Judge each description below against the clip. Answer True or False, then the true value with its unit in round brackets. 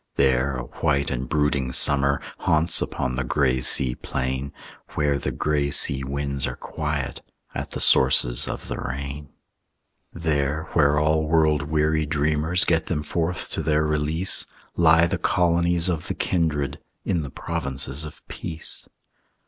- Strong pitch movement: False (2.4 semitones)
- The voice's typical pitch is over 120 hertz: False (75 Hz)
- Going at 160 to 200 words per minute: False (150 wpm)